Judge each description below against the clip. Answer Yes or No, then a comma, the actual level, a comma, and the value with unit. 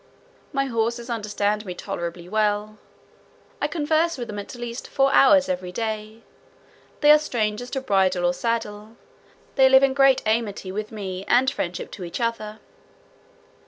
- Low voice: No, high, 220 Hz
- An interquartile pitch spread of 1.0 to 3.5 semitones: No, average, 4.2 semitones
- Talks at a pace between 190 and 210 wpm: No, average, 155 wpm